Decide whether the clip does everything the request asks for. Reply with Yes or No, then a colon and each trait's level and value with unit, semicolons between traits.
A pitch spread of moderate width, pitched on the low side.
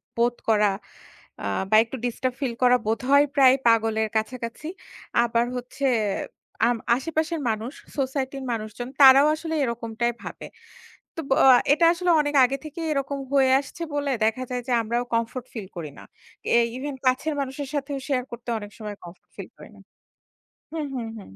No: average, 3.5 semitones; very high, 255 Hz